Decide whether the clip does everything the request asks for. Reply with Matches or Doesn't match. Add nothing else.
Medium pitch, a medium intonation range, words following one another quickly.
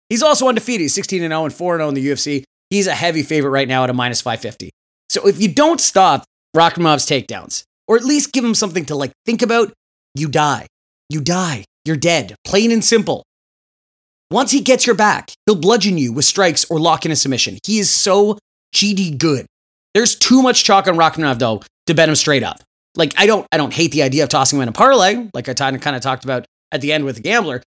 Doesn't match